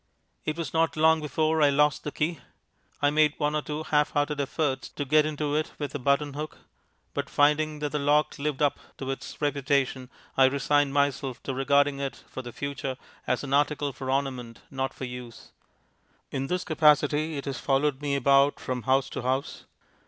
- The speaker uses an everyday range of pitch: No, narrow, 1.9 semitones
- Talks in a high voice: No, medium, 145 Hz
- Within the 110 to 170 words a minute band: No, average, 190 wpm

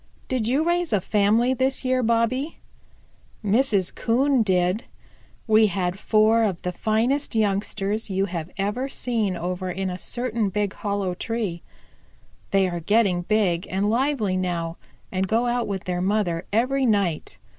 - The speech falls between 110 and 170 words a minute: Yes, average, 150 wpm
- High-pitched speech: Yes, high, 210 Hz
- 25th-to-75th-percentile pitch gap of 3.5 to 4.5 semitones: Yes, average, 4.0 semitones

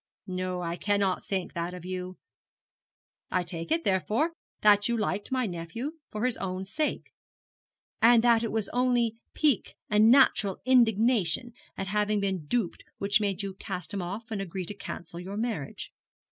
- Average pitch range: Yes, average, 4.0 semitones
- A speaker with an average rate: Yes, average, 165 wpm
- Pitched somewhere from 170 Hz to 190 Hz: No, high, 205 Hz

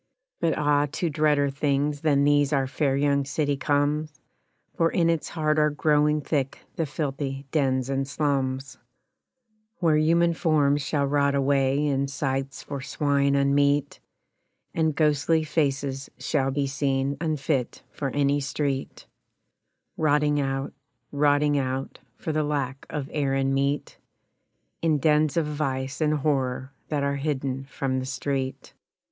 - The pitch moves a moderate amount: No, narrow, 1.7 semitones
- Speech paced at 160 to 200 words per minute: No, average, 140 wpm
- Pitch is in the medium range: Yes, medium, 145 Hz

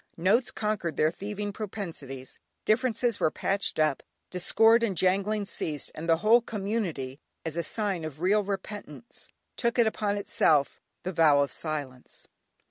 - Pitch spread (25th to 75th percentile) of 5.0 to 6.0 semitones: Yes, average, 5.3 semitones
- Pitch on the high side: Yes, high, 195 Hz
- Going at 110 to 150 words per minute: Yes, average, 140 wpm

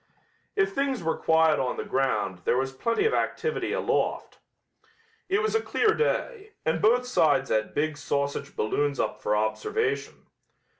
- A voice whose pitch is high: No, medium, 160 Hz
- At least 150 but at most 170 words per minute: Yes, average, 155 wpm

